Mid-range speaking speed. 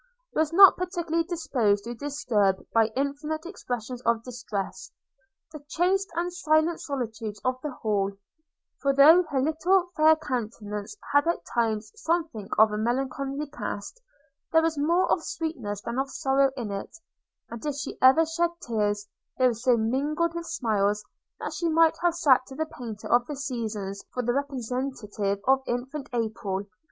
Yes: average, 160 wpm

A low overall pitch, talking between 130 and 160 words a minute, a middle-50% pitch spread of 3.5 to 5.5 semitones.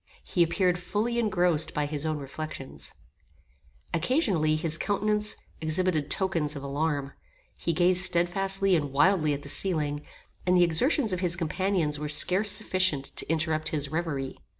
No: medium, 165 Hz; average, 150 wpm; average, 3.8 semitones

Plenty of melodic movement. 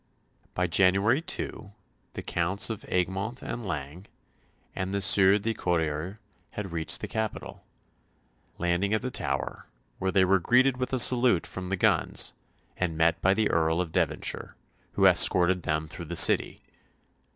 No: average, 3.5 semitones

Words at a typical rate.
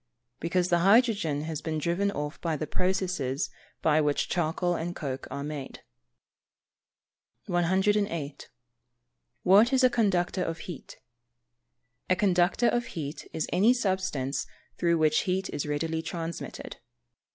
No: slow, 130 wpm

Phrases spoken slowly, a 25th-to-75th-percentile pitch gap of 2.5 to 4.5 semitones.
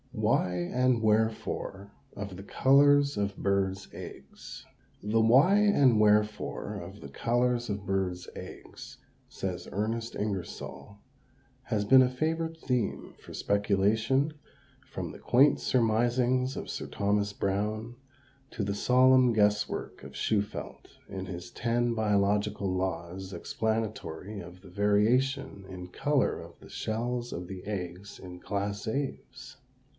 Yes: slow, 130 wpm; average, 4.0 semitones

